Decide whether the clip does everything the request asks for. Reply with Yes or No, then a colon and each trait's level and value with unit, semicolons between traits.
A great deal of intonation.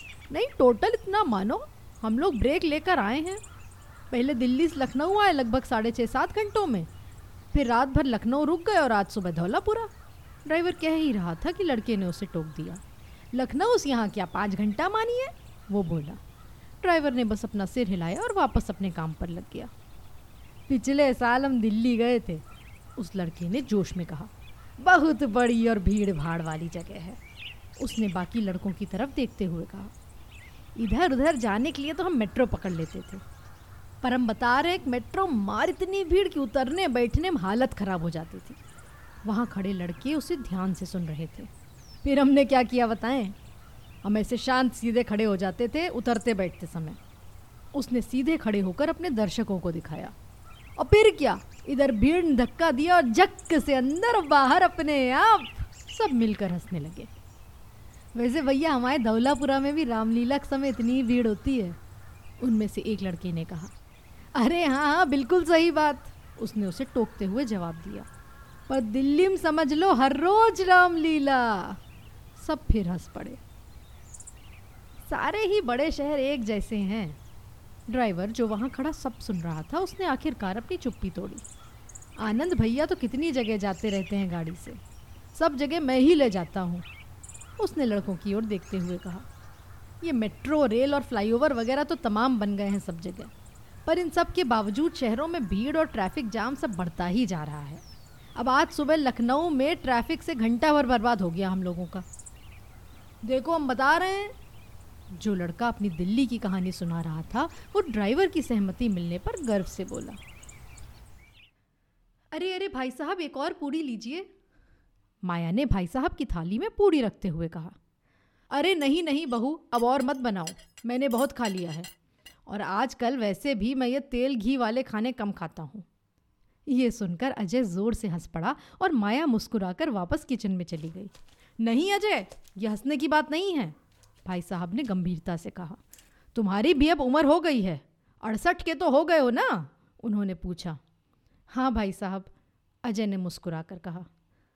Yes: wide, 7.7 semitones